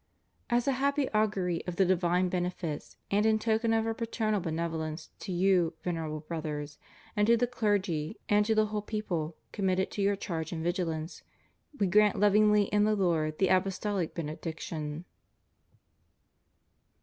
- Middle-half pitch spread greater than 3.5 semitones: Yes, average, 4.3 semitones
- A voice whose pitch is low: No, medium, 185 Hz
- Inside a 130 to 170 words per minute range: Yes, average, 160 wpm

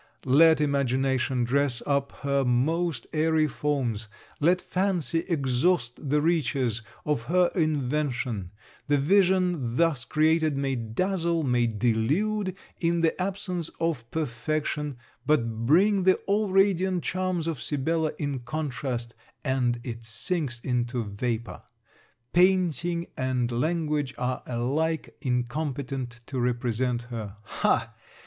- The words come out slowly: Yes, slow, 115 wpm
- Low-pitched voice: No, medium, 145 Hz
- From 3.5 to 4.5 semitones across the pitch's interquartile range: No, average, 5.3 semitones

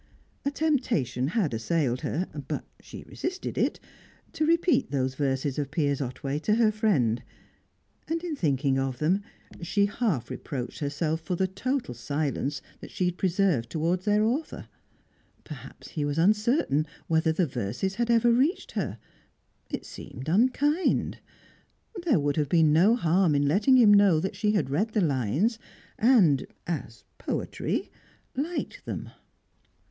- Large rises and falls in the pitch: Yes, wide, 7.6 semitones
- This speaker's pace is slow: No, average, 145 wpm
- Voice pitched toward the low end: No, medium, 170 Hz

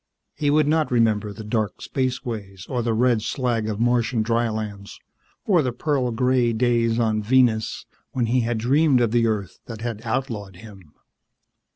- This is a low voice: Yes, low, 115 Hz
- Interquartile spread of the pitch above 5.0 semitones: No, narrow, 2.6 semitones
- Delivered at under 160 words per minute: No, average, 165 wpm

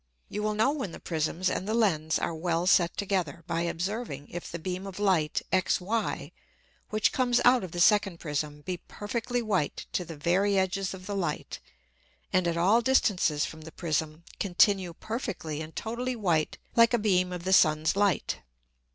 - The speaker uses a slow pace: No, average, 180 wpm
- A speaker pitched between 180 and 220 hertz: Yes, medium, 185 Hz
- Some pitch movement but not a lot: Yes, average, 4.0 semitones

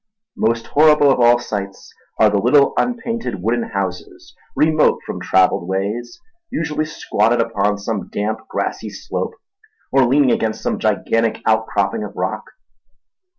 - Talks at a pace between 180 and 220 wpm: No, slow, 135 wpm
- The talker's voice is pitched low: Yes, low, 115 Hz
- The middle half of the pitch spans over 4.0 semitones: Yes, average, 5.0 semitones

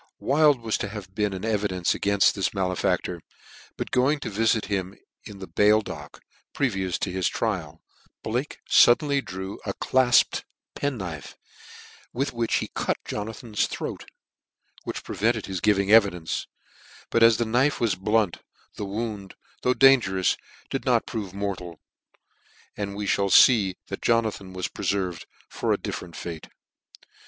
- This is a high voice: No, low, 105 Hz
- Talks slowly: No, average, 150 wpm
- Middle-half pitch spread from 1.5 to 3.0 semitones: No, average, 3.5 semitones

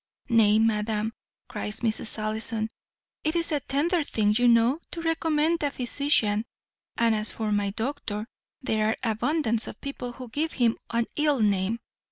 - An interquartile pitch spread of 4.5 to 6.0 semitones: Yes, average, 4.9 semitones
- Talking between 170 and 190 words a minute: No, average, 160 wpm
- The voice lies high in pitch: Yes, high, 230 Hz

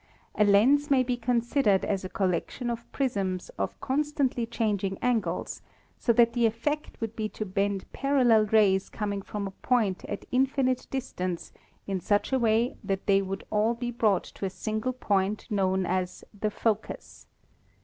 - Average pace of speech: Yes, average, 165 wpm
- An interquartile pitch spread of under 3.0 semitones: No, average, 3.9 semitones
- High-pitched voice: Yes, high, 215 Hz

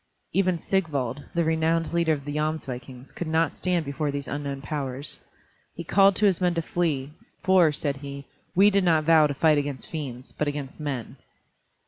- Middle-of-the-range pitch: Yes, medium, 155 Hz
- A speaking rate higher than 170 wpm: Yes, average, 180 wpm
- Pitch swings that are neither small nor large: Yes, average, 3.2 semitones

